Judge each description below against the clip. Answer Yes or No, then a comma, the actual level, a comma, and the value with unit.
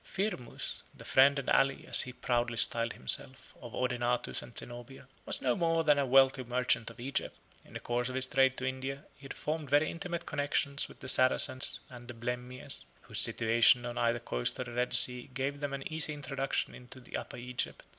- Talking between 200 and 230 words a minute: Yes, fast, 205 wpm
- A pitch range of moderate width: No, narrow, 2.2 semitones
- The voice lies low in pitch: Yes, low, 130 Hz